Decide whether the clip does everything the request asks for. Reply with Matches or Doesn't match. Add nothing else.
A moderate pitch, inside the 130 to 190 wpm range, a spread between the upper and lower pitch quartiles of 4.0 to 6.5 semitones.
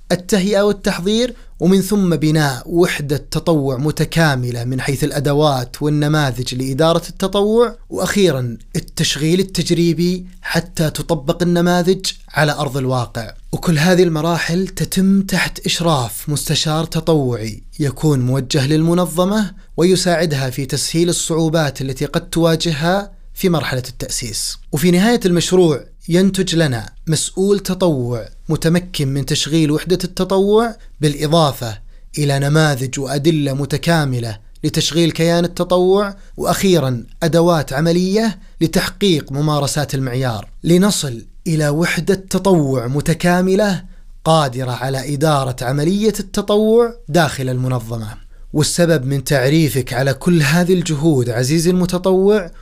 Doesn't match